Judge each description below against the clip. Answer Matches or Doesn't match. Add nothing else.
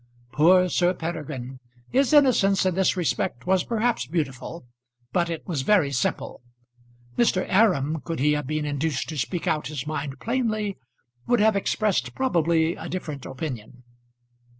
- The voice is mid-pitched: Matches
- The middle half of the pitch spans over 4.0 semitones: Matches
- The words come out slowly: Doesn't match